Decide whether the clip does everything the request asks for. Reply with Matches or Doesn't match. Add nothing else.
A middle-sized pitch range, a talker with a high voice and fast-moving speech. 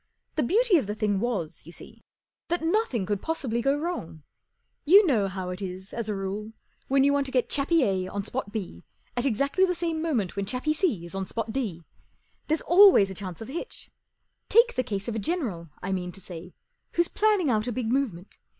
Doesn't match